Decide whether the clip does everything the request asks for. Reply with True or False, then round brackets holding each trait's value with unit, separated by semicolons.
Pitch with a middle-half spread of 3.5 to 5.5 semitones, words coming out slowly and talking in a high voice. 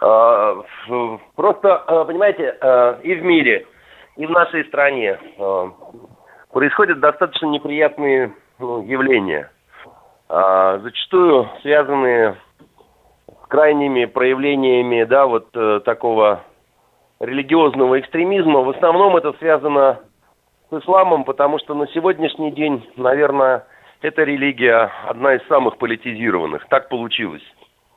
False (4.2 semitones; 90 wpm; 140 Hz)